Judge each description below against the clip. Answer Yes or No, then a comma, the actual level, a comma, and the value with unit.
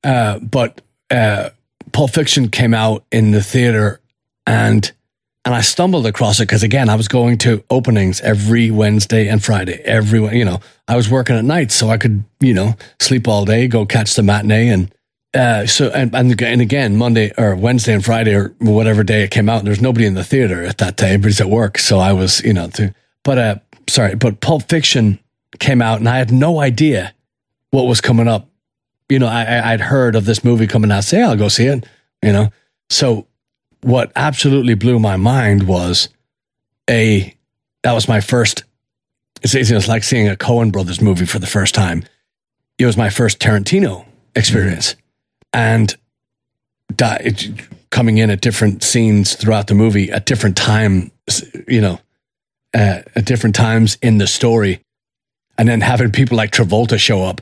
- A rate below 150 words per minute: No, average, 185 wpm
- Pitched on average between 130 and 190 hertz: No, low, 115 Hz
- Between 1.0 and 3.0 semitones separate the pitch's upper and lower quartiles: Yes, narrow, 2.6 semitones